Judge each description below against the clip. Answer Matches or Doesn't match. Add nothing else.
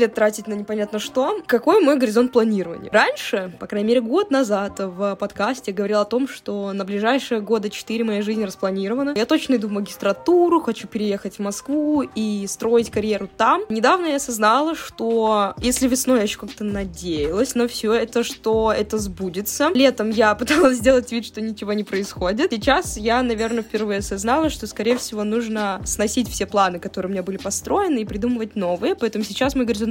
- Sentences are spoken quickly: Matches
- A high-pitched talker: Matches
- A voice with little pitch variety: Doesn't match